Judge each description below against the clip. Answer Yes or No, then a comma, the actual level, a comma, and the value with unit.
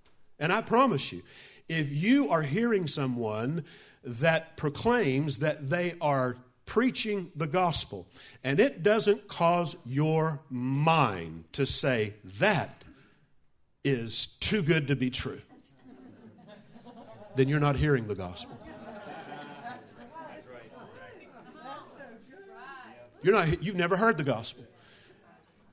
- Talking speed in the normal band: No, slow, 105 wpm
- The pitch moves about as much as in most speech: No, wide, 6.2 semitones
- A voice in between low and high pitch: Yes, medium, 150 Hz